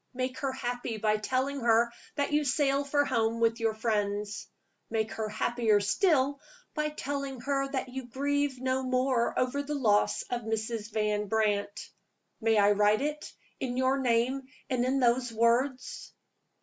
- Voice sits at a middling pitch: No, high, 245 Hz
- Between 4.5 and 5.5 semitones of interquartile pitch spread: No, average, 3.5 semitones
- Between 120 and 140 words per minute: No, average, 160 wpm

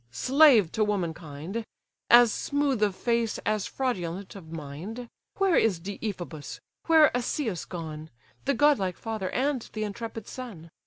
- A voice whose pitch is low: No, high, 215 Hz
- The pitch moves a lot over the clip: Yes, wide, 6.3 semitones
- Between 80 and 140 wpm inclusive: Yes, slow, 135 wpm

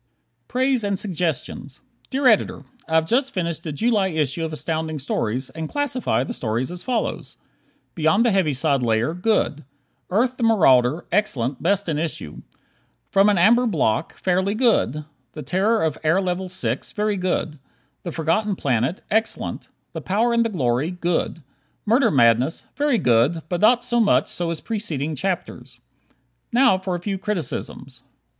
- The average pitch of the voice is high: No, medium, 175 Hz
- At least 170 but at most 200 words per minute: No, average, 160 wpm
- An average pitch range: No, wide, 6.1 semitones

